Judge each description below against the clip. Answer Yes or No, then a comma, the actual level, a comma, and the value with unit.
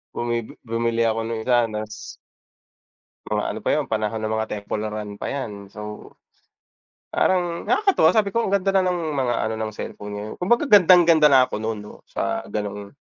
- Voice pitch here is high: No, low, 115 Hz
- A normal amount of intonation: No, wide, 8.2 semitones